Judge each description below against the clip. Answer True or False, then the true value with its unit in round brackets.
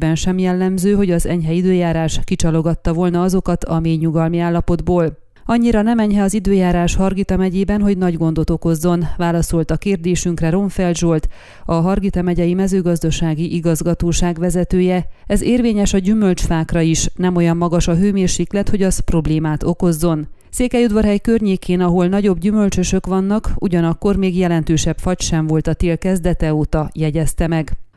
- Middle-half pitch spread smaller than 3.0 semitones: True (2.5 semitones)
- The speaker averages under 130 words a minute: False (145 wpm)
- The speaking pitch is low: False (175 Hz)